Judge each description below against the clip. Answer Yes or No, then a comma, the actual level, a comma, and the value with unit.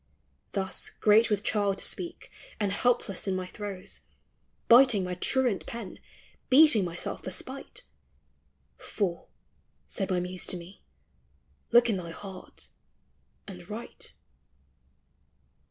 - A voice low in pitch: No, high, 200 Hz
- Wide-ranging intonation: No, average, 3.9 semitones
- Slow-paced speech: Yes, slow, 120 wpm